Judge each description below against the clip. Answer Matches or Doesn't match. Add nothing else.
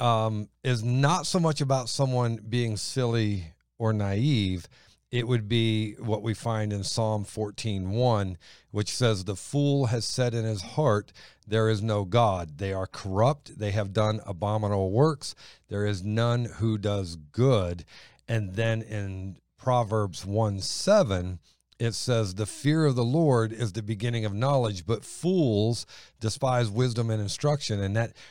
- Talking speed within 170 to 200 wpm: Doesn't match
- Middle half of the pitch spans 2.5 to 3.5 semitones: Matches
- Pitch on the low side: Matches